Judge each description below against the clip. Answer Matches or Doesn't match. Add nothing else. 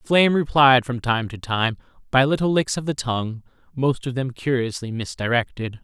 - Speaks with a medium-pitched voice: Doesn't match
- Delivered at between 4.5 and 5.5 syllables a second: Matches